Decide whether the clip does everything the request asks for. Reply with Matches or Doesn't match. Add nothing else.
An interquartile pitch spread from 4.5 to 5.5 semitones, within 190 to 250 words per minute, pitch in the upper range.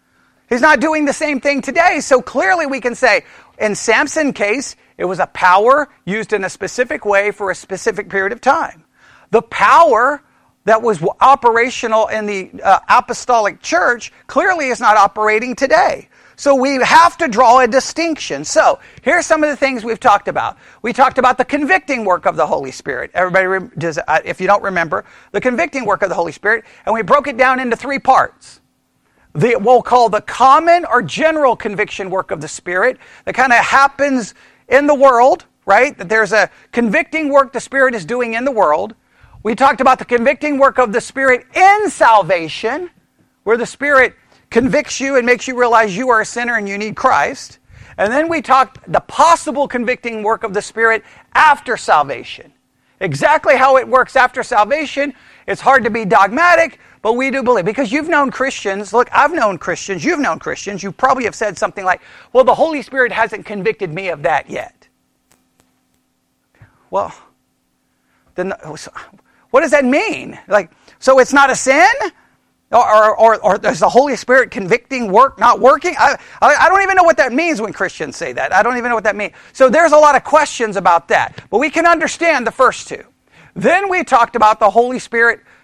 Matches